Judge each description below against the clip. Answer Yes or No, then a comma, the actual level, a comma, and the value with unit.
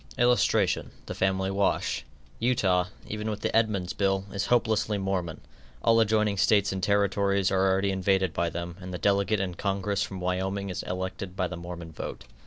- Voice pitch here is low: Yes, very low, 95 Hz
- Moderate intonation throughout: No, narrow, 1.8 semitones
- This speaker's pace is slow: No, average, 175 wpm